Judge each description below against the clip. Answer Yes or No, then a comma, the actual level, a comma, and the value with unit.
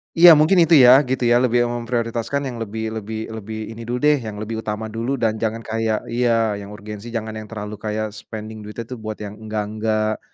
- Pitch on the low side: Yes, low, 110 Hz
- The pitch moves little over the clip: Yes, narrow, 1.9 semitones